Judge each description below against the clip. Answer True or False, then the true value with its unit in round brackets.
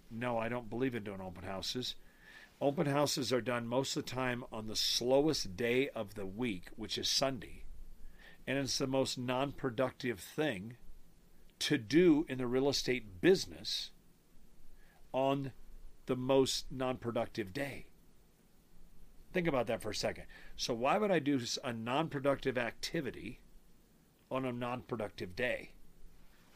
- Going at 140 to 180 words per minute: True (150 wpm)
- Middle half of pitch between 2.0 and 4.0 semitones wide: True (3.1 semitones)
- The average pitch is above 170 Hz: False (125 Hz)